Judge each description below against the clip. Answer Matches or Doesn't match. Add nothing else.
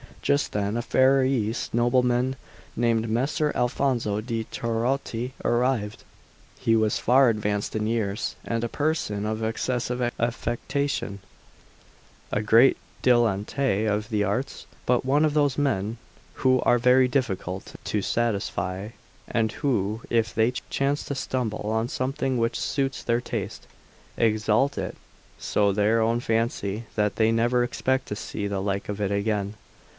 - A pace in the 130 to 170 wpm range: Matches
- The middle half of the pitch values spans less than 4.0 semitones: Matches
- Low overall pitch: Matches